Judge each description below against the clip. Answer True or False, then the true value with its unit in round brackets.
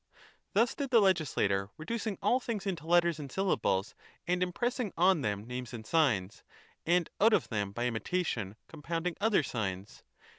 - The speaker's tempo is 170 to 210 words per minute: False (155 wpm)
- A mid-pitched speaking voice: True (165 Hz)